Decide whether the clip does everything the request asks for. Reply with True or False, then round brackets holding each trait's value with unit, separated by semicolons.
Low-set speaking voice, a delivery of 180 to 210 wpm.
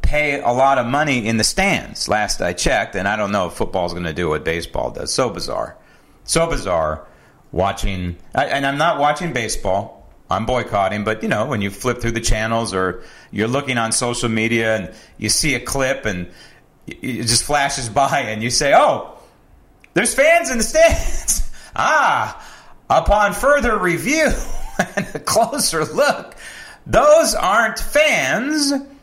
False (125 Hz; 165 wpm)